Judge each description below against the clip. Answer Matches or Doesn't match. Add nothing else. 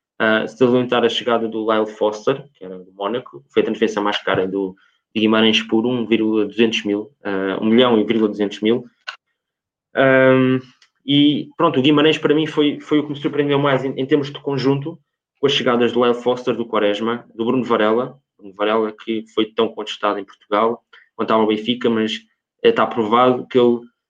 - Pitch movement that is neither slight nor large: Matches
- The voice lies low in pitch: Matches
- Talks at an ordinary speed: Doesn't match